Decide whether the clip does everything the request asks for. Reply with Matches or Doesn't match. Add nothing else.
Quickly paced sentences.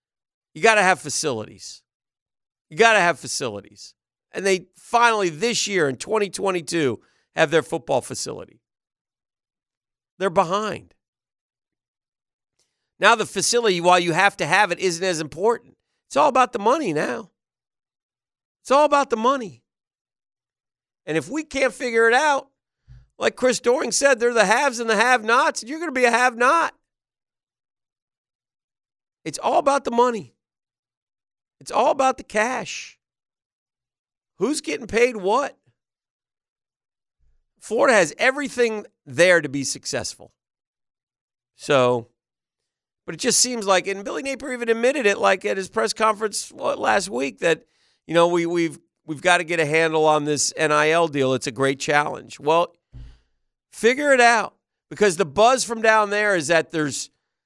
Doesn't match